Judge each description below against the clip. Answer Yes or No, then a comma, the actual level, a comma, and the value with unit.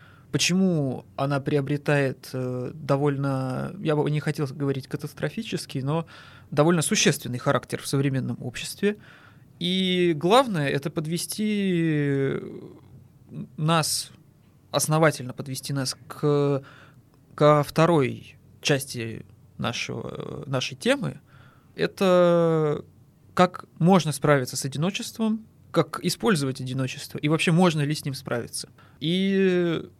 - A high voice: No, medium, 150 Hz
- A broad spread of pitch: No, average, 4.0 semitones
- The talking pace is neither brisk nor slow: No, slow, 100 wpm